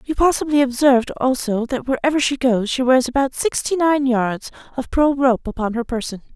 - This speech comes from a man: No, female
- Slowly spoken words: No, average, 190 wpm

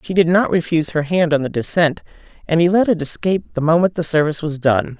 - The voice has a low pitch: No, medium, 165 Hz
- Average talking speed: No, fast, 240 wpm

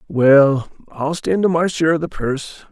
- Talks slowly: No, average, 200 wpm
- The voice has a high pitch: No, medium, 155 Hz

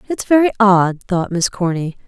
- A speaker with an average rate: Yes, average, 175 wpm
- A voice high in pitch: Yes, high, 195 Hz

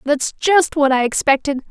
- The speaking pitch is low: No, very high, 285 Hz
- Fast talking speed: No, average, 175 wpm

